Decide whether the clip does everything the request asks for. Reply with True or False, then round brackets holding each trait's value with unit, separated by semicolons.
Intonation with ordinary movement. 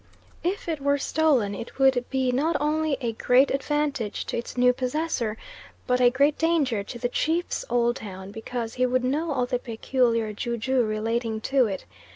True (3.6 semitones)